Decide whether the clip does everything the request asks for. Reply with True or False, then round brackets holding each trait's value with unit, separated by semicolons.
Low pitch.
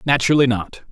True (130 Hz)